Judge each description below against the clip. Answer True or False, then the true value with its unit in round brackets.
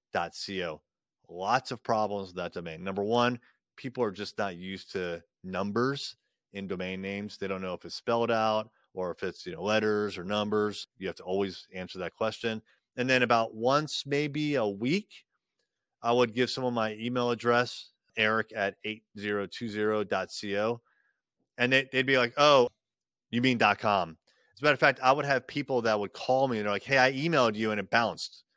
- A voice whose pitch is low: True (110 Hz)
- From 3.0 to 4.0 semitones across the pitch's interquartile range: True (3.6 semitones)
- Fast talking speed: False (190 wpm)